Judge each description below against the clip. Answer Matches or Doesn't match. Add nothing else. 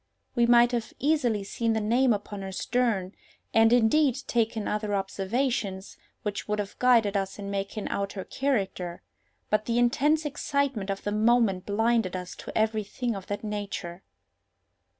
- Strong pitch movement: Doesn't match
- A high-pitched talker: Matches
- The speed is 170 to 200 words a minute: Doesn't match